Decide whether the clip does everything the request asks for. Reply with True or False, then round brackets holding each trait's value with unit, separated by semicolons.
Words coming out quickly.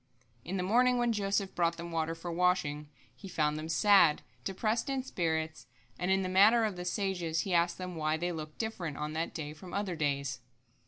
True (210 wpm)